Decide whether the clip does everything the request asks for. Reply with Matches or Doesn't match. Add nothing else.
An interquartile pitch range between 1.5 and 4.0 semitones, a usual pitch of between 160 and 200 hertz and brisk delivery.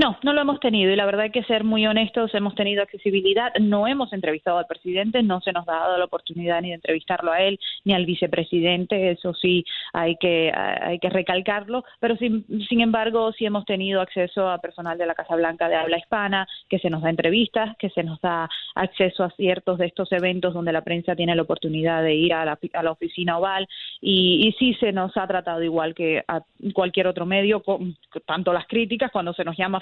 Matches